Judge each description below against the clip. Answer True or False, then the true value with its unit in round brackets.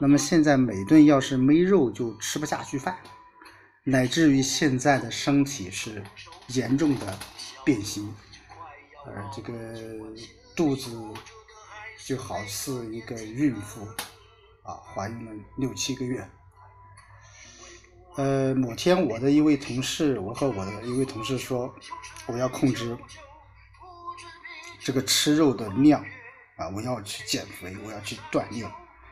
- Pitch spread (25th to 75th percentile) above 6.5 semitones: False (5.3 semitones)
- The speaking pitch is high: False (125 Hz)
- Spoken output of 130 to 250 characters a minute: True (185 characters per minute)